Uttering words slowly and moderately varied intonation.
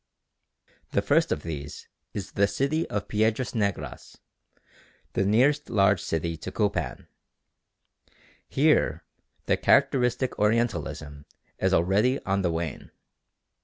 No: slow, 110 wpm; wide, 5.8 semitones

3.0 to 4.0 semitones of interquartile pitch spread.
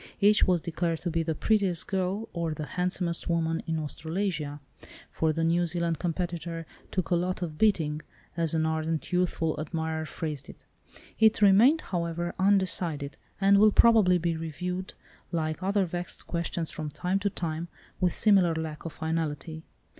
No: narrow, 2.5 semitones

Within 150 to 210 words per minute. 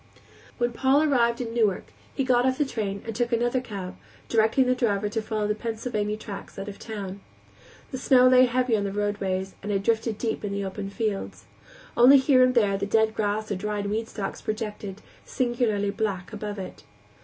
Yes: average, 200 wpm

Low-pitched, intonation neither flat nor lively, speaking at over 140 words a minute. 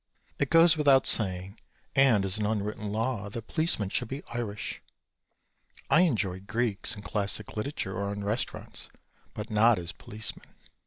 Yes: low, 105 Hz; average, 3.3 semitones; average, 150 wpm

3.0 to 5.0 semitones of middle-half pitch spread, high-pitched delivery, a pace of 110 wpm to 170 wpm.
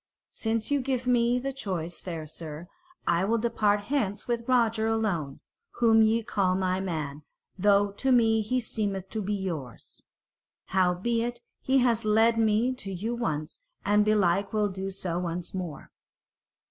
Yes: average, 4.1 semitones; high, 210 Hz; average, 155 wpm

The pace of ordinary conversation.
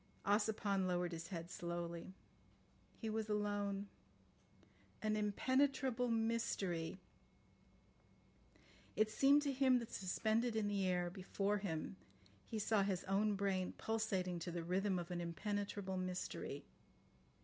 No: slow, 125 wpm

